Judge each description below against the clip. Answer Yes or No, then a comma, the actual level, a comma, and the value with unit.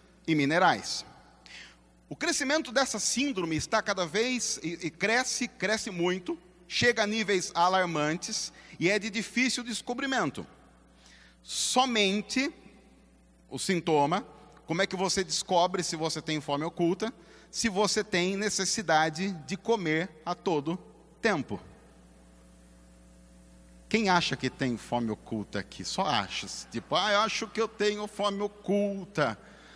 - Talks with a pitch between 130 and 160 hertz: No, medium, 185 Hz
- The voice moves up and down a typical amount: No, wide, 6.0 semitones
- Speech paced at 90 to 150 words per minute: Yes, average, 125 wpm